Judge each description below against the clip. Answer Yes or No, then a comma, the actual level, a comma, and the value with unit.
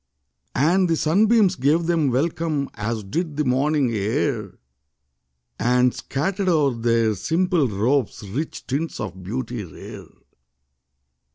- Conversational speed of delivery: No, slow, 115 wpm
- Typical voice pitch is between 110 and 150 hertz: Yes, medium, 140 Hz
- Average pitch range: No, wide, 5.9 semitones